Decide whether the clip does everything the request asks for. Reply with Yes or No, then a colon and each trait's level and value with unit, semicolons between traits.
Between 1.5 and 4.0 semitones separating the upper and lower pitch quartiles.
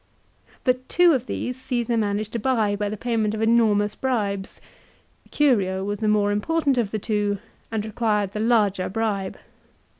Yes: average, 2.8 semitones